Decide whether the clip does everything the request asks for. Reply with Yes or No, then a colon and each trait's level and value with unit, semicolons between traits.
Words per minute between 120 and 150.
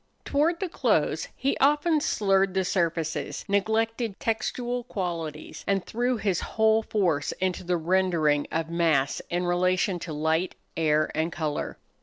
Yes: average, 140 wpm